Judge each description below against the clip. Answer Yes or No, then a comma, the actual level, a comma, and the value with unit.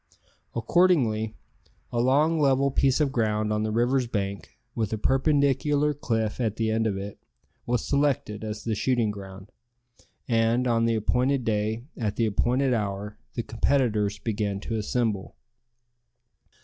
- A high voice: No, low, 115 Hz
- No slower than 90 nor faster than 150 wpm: Yes, average, 145 wpm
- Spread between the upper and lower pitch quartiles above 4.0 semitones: No, average, 3.7 semitones